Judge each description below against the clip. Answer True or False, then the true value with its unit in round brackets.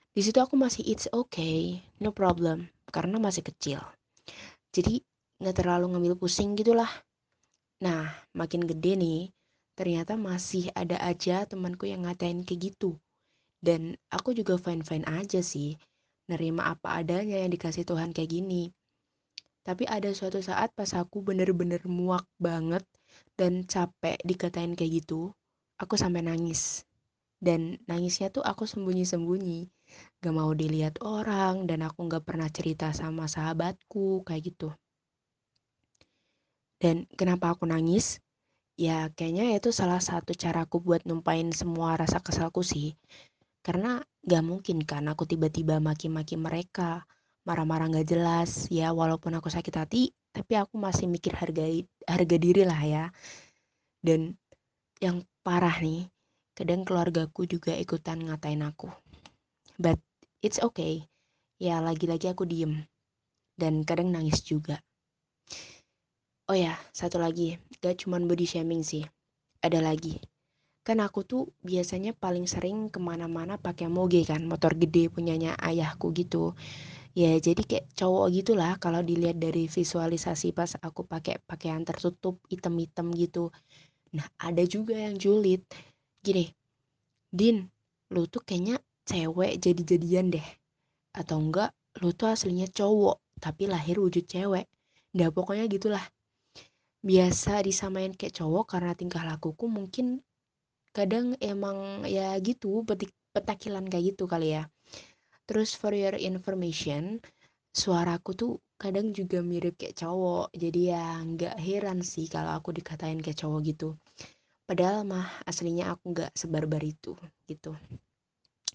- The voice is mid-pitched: True (175 Hz)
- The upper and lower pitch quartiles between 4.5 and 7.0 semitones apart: False (2.5 semitones)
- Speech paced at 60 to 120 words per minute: False (130 wpm)